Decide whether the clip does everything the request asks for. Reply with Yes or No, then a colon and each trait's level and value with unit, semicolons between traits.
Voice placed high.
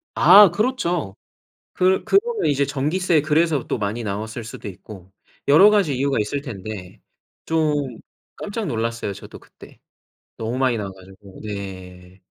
No: low, 125 Hz